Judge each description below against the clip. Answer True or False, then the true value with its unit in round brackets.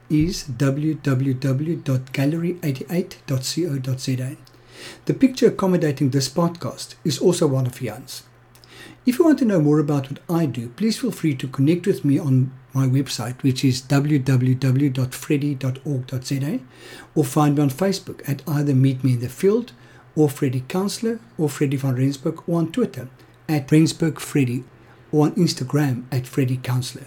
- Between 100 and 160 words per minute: True (145 wpm)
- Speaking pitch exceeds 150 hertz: False (140 Hz)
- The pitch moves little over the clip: False (3.7 semitones)